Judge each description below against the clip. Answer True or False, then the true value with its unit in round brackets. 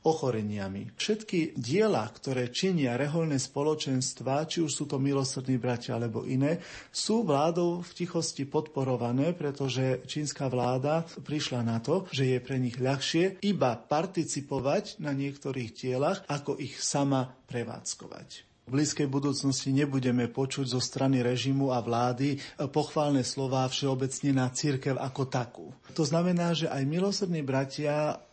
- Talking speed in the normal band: True (135 wpm)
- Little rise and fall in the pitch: False (3.0 semitones)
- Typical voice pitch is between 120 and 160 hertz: True (140 Hz)